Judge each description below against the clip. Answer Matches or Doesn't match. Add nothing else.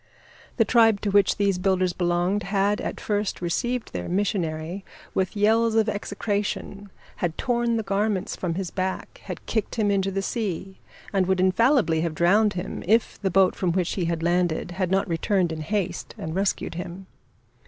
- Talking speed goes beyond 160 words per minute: Matches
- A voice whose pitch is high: Matches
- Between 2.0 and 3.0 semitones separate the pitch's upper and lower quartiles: Matches